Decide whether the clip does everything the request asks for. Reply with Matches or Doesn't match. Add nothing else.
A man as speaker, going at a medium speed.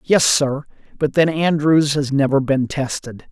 Matches